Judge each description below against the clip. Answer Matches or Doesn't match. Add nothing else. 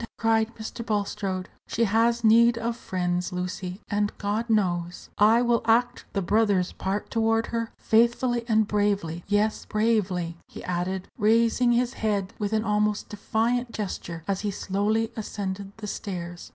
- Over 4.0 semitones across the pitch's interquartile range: Doesn't match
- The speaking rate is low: Doesn't match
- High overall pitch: Matches